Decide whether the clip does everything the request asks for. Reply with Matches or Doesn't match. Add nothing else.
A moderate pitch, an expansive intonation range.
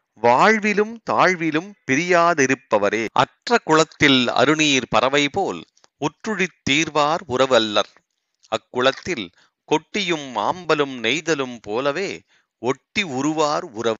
Doesn't match